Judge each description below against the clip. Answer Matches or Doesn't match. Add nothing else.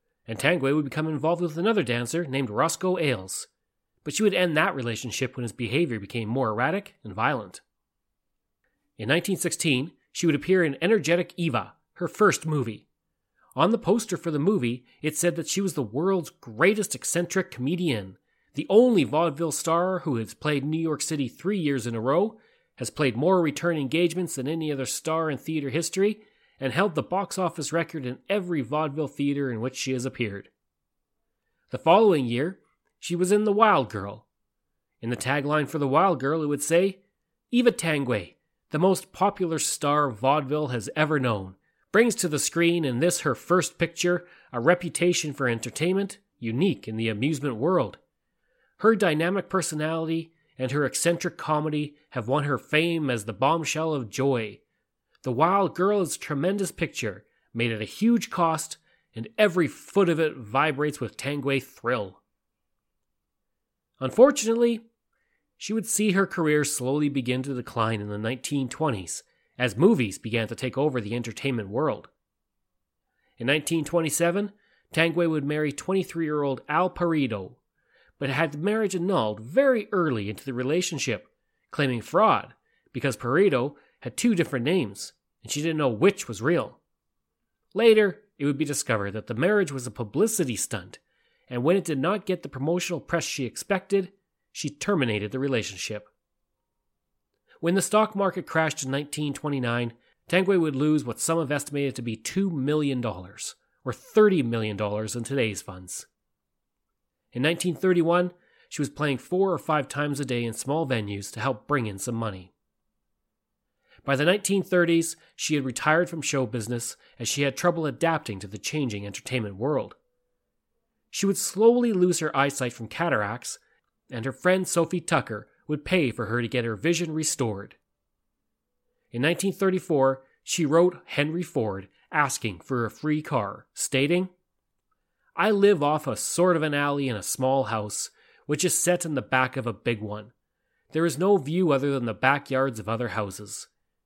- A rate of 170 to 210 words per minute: Doesn't match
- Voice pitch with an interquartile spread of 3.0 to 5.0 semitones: Doesn't match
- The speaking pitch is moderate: Matches